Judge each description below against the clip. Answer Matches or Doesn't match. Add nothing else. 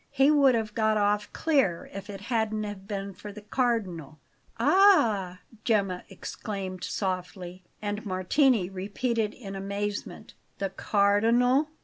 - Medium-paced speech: Doesn't match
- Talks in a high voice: Matches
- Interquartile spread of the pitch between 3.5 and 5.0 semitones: Doesn't match